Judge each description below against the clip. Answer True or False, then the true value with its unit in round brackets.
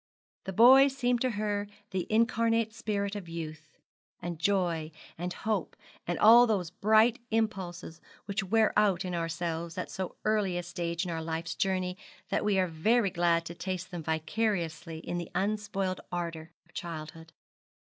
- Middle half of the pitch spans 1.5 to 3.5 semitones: False (4.1 semitones)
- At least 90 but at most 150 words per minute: False (160 wpm)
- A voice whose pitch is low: False (185 Hz)